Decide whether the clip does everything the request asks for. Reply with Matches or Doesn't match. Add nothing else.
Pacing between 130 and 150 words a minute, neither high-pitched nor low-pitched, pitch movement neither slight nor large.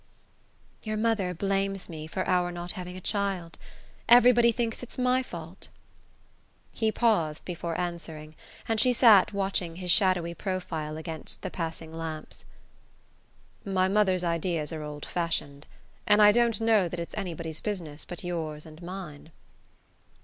Matches